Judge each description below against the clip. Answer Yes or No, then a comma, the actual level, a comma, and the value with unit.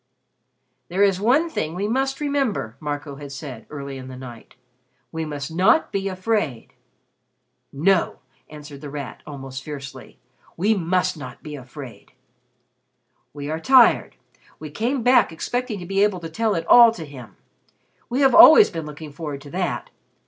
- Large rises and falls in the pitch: Yes, wide, 6.9 semitones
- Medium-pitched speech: Yes, medium, 160 Hz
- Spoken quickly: No, average, 160 wpm